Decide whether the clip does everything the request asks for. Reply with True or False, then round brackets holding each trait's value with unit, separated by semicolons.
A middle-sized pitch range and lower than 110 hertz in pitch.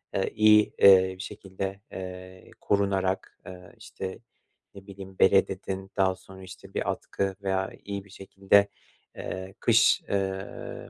False (0.8 semitones; 95 Hz)